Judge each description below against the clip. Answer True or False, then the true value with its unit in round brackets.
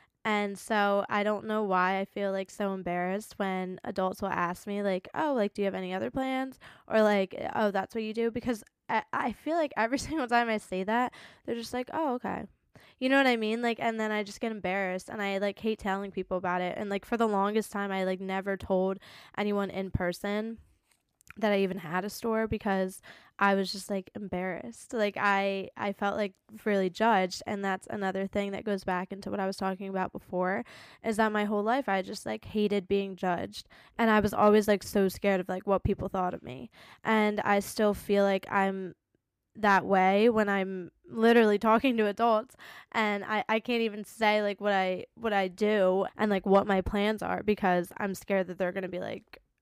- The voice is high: True (200 Hz)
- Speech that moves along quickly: True (220 wpm)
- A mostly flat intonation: True (2.3 semitones)